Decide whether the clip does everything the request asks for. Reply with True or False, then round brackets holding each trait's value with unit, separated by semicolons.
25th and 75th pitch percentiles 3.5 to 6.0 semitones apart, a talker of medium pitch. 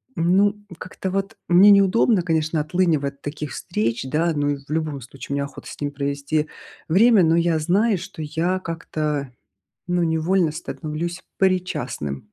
True (3.9 semitones; 160 Hz)